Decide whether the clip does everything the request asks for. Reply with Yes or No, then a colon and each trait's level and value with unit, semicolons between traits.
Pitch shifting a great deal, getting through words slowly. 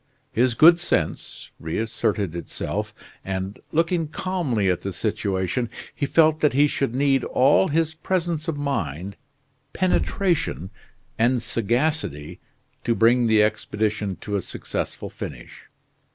Yes: wide, 7.5 semitones; slow, 125 wpm